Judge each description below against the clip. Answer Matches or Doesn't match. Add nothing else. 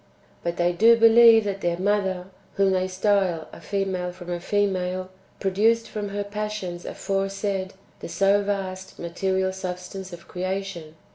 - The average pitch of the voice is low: Doesn't match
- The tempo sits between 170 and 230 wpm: Doesn't match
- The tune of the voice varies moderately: Doesn't match